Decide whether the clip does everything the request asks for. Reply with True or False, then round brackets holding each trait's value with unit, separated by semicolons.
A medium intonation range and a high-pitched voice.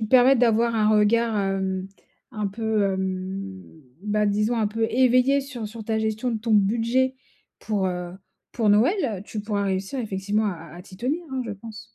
True (3.0 semitones; 215 Hz)